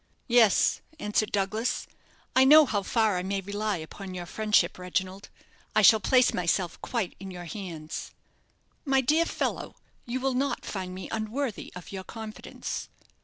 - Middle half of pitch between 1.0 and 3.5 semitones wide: No, average, 4.4 semitones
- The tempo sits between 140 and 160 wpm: Yes, average, 155 wpm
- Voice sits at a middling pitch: No, high, 205 Hz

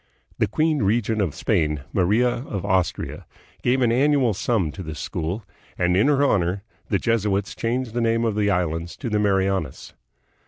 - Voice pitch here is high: No, low, 105 Hz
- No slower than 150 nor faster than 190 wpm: Yes, average, 170 wpm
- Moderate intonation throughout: Yes, average, 4.7 semitones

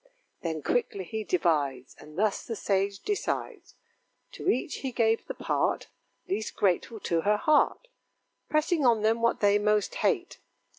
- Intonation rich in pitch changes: No, average, 4.3 semitones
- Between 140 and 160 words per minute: Yes, average, 150 wpm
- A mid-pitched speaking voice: No, high, 210 Hz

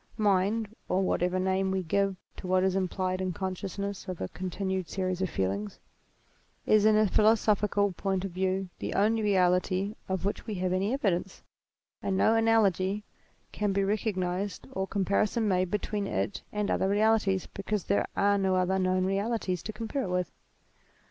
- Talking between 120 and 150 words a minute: No, average, 175 wpm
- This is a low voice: No, high, 195 Hz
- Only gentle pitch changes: Yes, narrow, 2.0 semitones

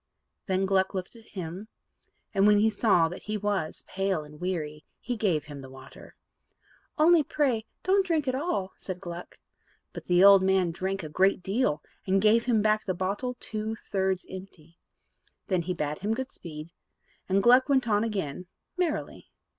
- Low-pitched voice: No, high, 195 Hz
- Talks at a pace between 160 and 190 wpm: Yes, average, 175 wpm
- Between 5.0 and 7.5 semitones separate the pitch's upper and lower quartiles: No, average, 3.8 semitones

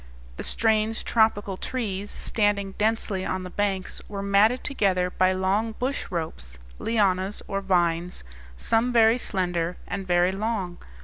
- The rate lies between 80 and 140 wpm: Yes, slow, 135 wpm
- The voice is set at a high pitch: Yes, high, 195 Hz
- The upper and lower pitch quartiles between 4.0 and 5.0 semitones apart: No, average, 3.0 semitones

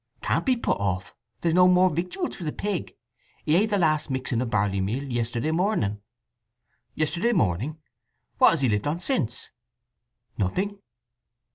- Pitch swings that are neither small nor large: No, wide, 8.2 semitones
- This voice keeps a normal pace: Yes, average, 150 wpm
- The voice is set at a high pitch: No, medium, 150 Hz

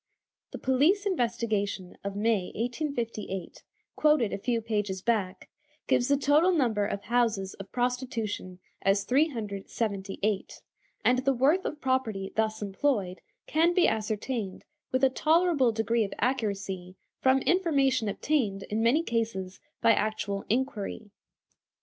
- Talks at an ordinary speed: No, slow, 125 wpm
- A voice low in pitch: No, high, 230 Hz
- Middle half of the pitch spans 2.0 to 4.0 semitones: No, average, 4.7 semitones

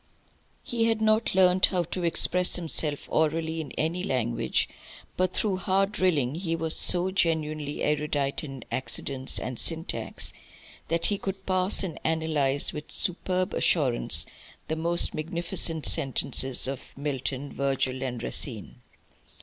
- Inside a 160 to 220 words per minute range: No, slow, 135 wpm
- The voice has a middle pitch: Yes, medium, 160 Hz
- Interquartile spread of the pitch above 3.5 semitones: Yes, average, 4.7 semitones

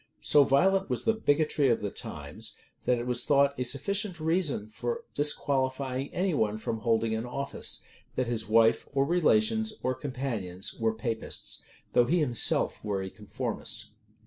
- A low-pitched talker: Yes, low, 130 Hz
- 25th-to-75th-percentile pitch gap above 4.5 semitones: Yes, average, 5.1 semitones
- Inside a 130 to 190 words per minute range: Yes, average, 160 wpm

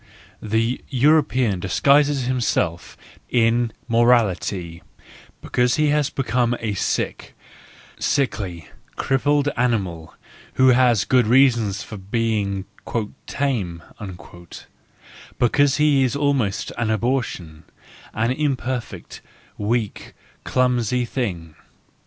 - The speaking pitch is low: Yes, low, 120 Hz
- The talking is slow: Yes, slow, 100 wpm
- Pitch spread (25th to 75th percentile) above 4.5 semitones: No, average, 4.2 semitones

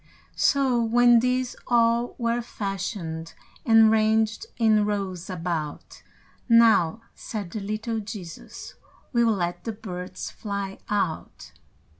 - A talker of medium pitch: No, high, 215 Hz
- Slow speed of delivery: Yes, slow, 110 wpm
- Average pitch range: Yes, average, 3.7 semitones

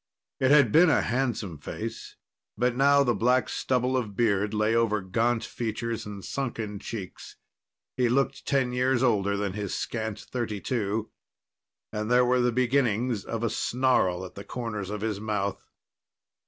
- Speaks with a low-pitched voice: Yes, low, 115 Hz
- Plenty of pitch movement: No, average, 3.2 semitones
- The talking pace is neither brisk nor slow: Yes, average, 160 wpm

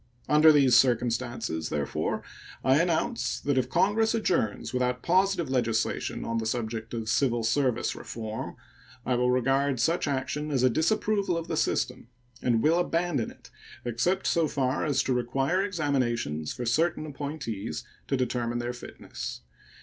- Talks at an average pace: Yes, average, 150 wpm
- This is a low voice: Yes, low, 130 Hz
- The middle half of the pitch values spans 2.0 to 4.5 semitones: No, average, 4.9 semitones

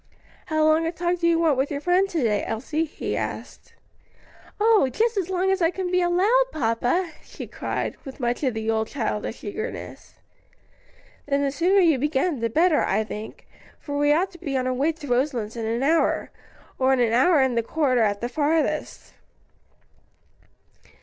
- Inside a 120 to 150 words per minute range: No, average, 185 wpm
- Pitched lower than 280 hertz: No, very high, 295 Hz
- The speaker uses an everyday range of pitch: No, wide, 5.9 semitones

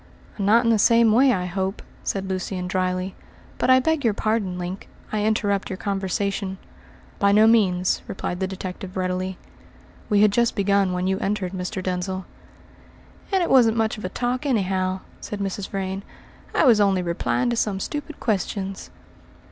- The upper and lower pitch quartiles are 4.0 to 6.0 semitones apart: No, average, 2.9 semitones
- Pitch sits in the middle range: No, high, 195 Hz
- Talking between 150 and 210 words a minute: Yes, average, 170 wpm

